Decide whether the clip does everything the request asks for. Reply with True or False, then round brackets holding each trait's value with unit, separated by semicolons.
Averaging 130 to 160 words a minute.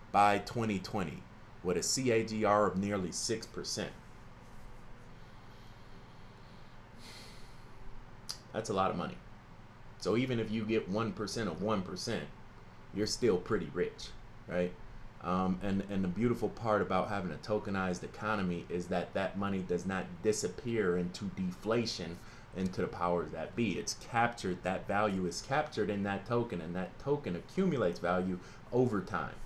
True (135 wpm)